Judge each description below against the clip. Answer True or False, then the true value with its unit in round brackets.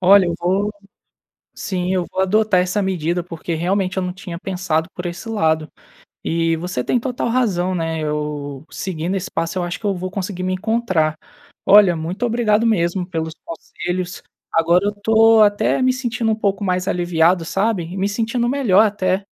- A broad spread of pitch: False (3.4 semitones)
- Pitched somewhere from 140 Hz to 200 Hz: True (185 Hz)